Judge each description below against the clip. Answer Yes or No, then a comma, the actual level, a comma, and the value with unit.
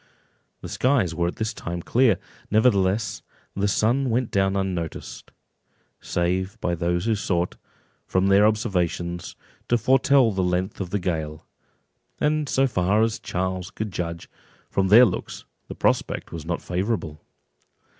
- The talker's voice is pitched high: No, very low, 95 Hz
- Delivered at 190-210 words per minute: No, average, 145 wpm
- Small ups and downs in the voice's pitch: No, average, 4.0 semitones